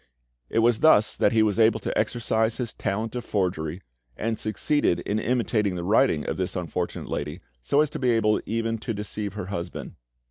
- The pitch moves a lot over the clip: No, average, 3.0 semitones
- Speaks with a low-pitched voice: Yes, low, 110 Hz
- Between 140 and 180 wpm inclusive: No, average, 190 wpm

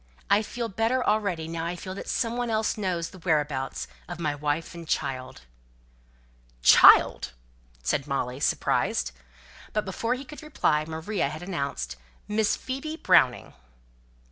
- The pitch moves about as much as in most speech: No, wide, 6.8 semitones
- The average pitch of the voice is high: No, medium, 175 Hz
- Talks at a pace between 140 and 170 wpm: Yes, average, 145 wpm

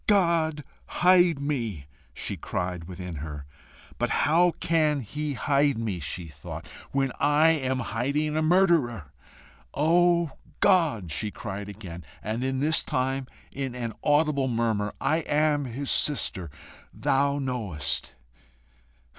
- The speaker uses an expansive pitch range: Yes, wide, 6.7 semitones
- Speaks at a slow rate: Yes, slow, 120 wpm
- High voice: No, low, 135 Hz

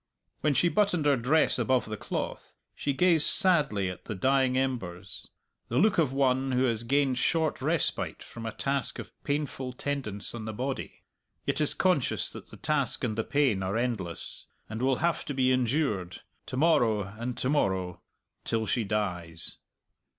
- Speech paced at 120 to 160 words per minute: No, average, 170 wpm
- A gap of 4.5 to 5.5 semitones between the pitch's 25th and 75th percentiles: Yes, average, 4.9 semitones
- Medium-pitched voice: No, low, 130 Hz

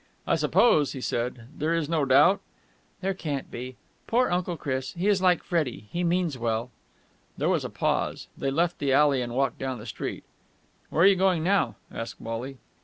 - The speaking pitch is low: No, medium, 145 Hz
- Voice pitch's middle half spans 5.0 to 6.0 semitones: Yes, wide, 5.6 semitones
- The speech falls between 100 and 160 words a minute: No, average, 190 wpm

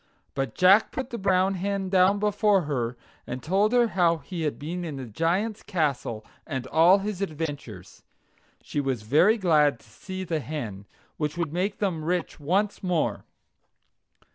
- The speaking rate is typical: Yes, average, 165 wpm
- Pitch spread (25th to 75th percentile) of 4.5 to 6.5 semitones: Yes, average, 5.1 semitones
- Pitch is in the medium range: Yes, medium, 170 Hz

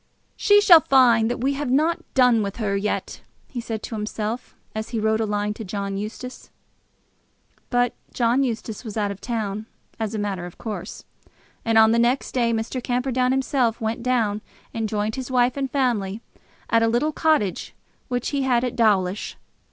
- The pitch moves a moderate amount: Yes, average, 3.0 semitones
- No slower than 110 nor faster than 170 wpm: No, average, 185 wpm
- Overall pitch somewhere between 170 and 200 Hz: No, high, 230 Hz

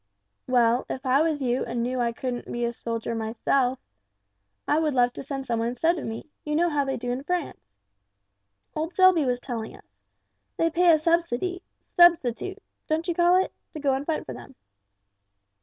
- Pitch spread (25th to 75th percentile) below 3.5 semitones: No, wide, 5.4 semitones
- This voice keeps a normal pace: Yes, average, 190 wpm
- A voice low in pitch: No, very high, 270 Hz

